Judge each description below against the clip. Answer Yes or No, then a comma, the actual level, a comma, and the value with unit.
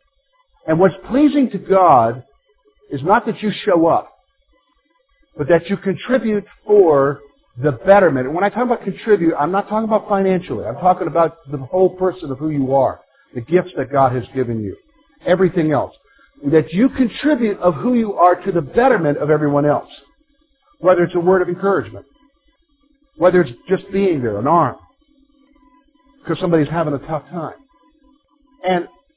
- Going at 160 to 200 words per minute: Yes, average, 165 wpm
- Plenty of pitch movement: Yes, wide, 8.6 semitones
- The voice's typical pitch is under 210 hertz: Yes, high, 190 Hz